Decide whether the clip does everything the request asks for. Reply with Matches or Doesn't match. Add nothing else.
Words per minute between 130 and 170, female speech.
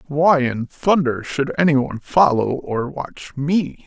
Doesn't match